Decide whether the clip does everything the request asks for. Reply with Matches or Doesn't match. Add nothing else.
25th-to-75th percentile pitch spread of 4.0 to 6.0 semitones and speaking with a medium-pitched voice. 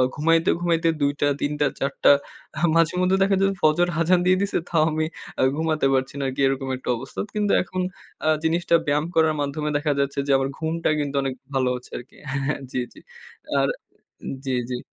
Doesn't match